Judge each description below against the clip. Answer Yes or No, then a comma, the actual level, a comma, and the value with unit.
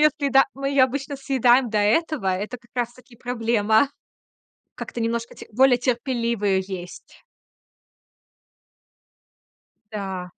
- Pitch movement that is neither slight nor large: Yes, average, 3.6 semitones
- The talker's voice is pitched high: Yes, high, 240 Hz